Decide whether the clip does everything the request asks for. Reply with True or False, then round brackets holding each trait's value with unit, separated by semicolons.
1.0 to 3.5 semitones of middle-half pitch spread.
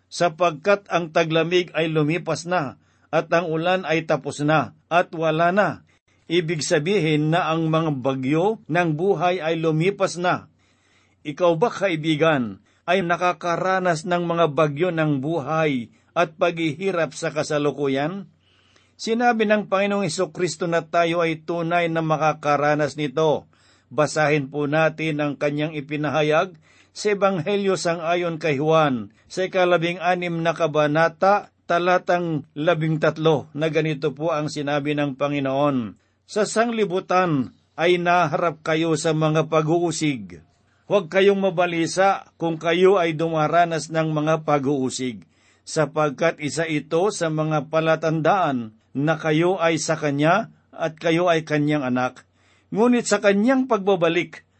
True (2.9 semitones)